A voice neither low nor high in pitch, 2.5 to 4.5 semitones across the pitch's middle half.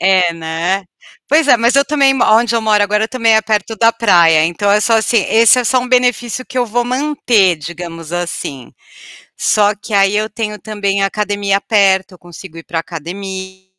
No: high, 205 Hz; average, 3.8 semitones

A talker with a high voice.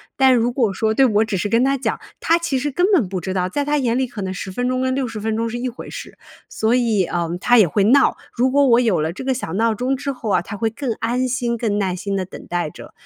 Yes: high, 230 Hz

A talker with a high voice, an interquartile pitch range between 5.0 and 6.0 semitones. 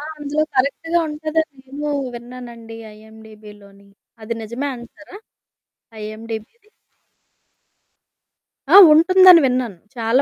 Yes: very high, 250 Hz; wide, 5.5 semitones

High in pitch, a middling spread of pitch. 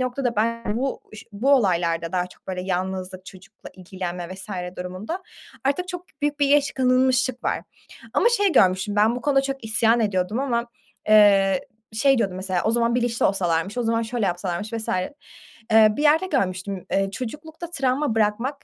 No: high, 220 Hz; wide, 5.8 semitones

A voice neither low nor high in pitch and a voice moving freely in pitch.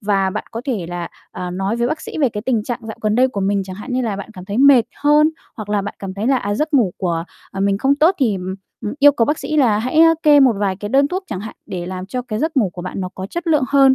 No: high, 220 Hz; wide, 5.8 semitones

